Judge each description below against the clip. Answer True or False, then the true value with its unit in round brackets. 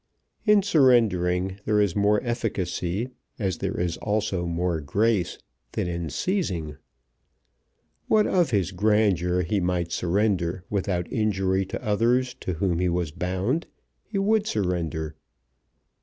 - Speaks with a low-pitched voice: True (95 Hz)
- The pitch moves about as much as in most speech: True (4.0 semitones)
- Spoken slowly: True (125 wpm)